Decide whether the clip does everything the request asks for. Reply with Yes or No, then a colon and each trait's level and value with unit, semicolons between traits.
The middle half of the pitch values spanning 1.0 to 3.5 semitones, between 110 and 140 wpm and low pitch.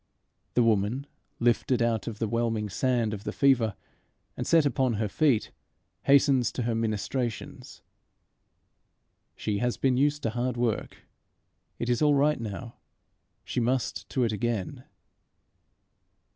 Yes: average, 2.9 semitones; slow, 135 wpm; low, 120 Hz